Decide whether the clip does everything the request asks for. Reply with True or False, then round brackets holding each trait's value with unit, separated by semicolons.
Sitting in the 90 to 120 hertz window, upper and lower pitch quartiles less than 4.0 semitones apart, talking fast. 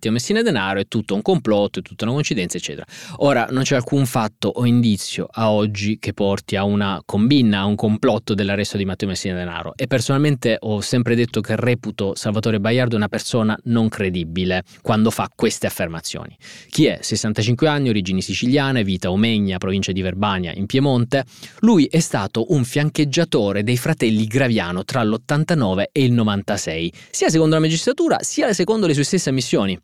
False (110 Hz; 5.2 semitones; 175 wpm)